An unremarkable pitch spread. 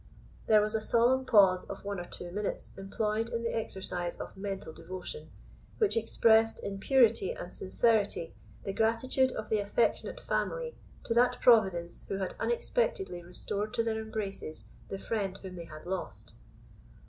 Yes: average, 3.2 semitones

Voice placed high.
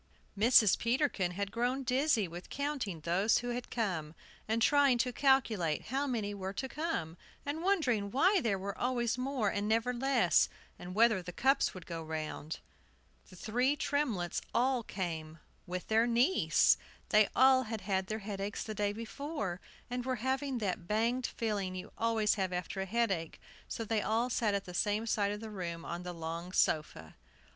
Yes: high, 220 Hz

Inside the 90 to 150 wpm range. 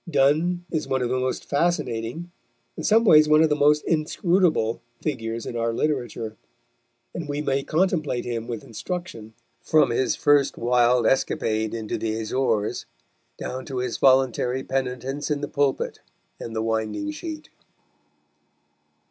Yes: average, 145 wpm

